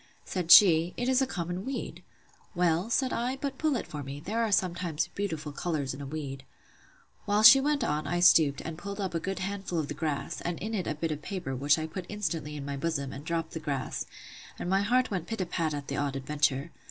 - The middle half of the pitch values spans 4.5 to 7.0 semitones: Yes, average, 5.2 semitones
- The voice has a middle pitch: Yes, medium, 170 Hz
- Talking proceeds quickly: Yes, fast, 240 wpm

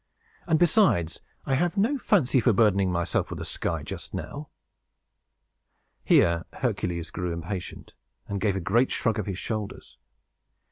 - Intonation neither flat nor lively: No, wide, 8.0 semitones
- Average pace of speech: Yes, average, 145 wpm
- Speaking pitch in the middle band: No, low, 105 Hz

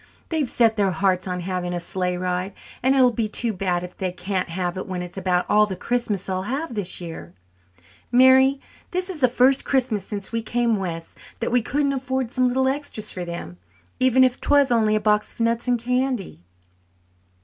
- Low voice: No, high, 215 Hz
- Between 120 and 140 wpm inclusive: No, fast, 205 wpm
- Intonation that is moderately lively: No, wide, 5.7 semitones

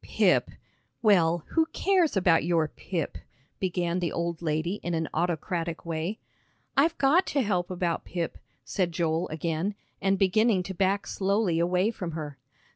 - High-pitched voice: No, medium, 175 Hz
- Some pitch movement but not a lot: Yes, average, 3.1 semitones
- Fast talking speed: No, average, 150 wpm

